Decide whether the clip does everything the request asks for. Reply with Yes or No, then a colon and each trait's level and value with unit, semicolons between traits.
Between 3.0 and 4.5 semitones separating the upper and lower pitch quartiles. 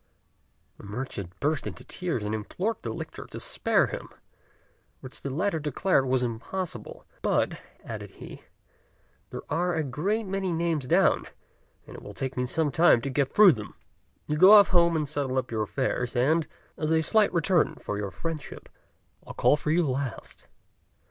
No: average, 5.2 semitones